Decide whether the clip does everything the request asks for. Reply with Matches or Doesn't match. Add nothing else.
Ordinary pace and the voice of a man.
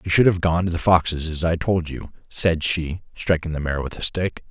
Doesn't match